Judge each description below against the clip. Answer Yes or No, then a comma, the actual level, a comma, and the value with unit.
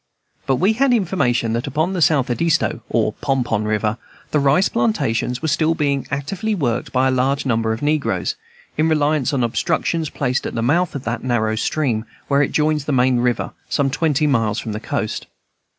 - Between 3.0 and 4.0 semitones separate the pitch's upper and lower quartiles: No, average, 4.6 semitones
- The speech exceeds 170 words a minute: Yes, average, 195 wpm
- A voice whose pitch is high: No, low, 135 Hz